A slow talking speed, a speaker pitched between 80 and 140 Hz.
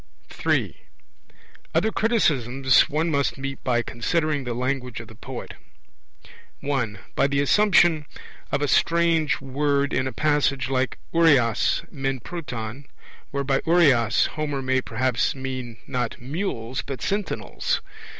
Yes: slow, 130 wpm; low, 135 Hz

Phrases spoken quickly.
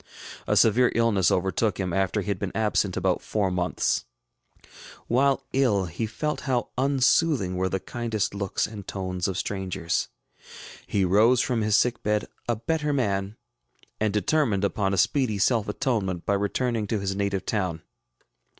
No: average, 160 wpm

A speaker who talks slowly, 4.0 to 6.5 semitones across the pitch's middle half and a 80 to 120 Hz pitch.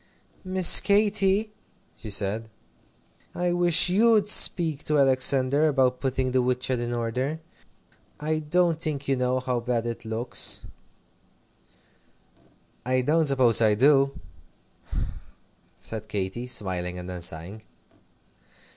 No: slow, 115 wpm; average, 5.2 semitones; low, 130 Hz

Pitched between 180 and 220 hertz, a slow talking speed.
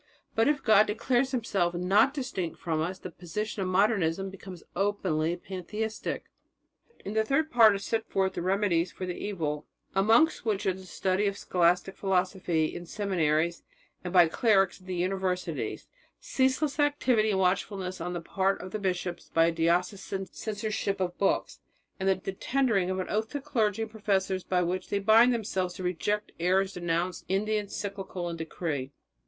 No: high, 190 Hz; average, 180 wpm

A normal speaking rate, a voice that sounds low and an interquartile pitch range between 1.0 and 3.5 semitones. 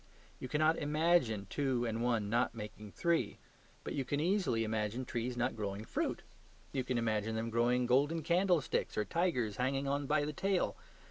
No: average, 175 wpm; low, 125 Hz; average, 5.1 semitones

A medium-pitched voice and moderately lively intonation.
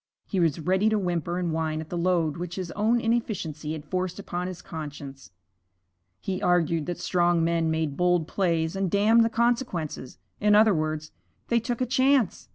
Yes: medium, 175 Hz; average, 4.3 semitones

